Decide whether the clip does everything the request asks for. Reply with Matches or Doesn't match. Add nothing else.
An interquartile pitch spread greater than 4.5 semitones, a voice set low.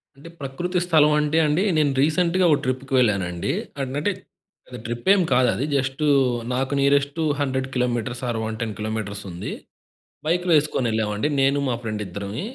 Matches